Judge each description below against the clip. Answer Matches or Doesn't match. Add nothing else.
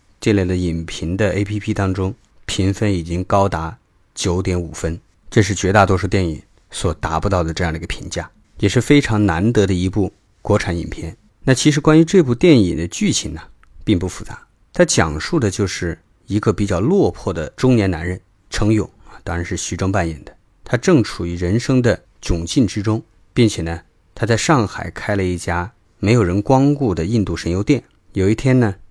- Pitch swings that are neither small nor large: Matches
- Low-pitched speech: Matches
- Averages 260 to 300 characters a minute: Matches